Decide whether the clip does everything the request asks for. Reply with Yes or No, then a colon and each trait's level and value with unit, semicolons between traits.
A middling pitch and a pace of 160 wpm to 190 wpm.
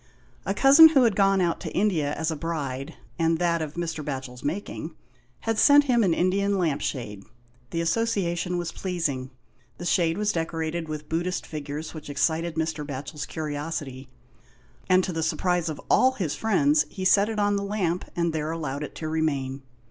Yes: medium, 165 Hz; average, 180 wpm